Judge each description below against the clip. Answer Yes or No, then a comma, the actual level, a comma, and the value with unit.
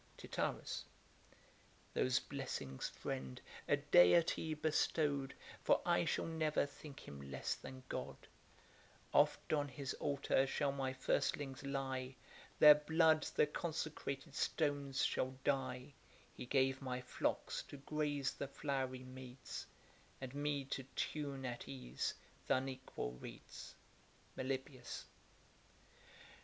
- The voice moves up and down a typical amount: No, narrow, 2.1 semitones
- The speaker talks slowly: Yes, slow, 115 wpm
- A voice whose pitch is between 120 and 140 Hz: Yes, low, 135 Hz